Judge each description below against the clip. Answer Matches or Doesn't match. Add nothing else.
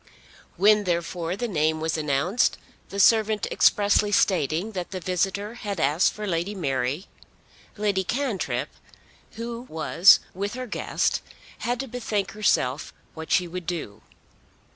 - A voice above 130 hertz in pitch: Matches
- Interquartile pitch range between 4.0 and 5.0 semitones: Matches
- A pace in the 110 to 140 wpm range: Matches